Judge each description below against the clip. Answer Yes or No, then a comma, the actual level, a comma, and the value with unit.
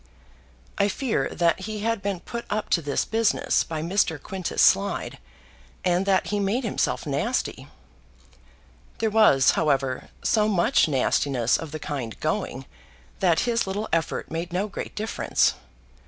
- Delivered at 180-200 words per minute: No, average, 145 wpm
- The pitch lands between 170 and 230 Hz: Yes, high, 190 Hz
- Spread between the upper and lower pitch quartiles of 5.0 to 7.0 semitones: Yes, average, 5.3 semitones